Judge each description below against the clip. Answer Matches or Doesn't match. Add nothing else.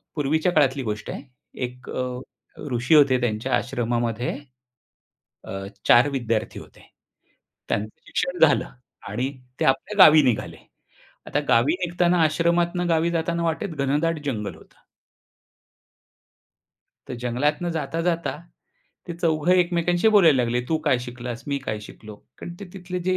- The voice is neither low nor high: Matches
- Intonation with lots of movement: Matches